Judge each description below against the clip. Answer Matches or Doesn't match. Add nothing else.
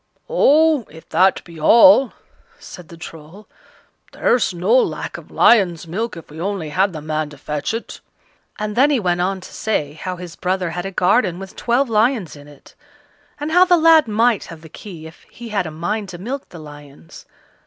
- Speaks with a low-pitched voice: Doesn't match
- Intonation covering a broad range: Matches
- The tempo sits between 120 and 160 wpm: Doesn't match